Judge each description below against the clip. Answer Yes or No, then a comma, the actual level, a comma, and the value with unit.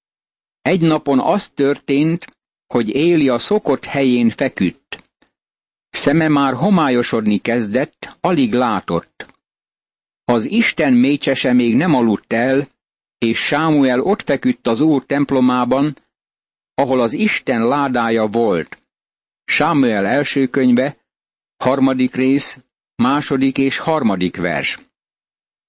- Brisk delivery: No, slow, 105 wpm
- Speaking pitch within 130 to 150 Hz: Yes, low, 135 Hz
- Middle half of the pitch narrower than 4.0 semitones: Yes, average, 2.8 semitones